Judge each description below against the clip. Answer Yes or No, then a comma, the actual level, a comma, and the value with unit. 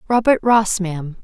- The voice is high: Yes, high, 200 Hz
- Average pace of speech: Yes, average, 145 wpm